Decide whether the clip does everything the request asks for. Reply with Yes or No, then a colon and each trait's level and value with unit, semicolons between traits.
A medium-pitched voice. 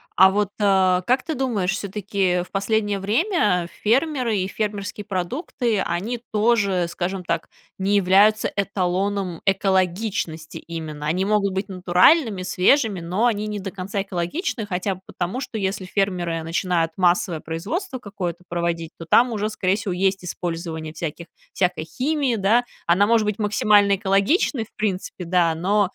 No: high, 195 Hz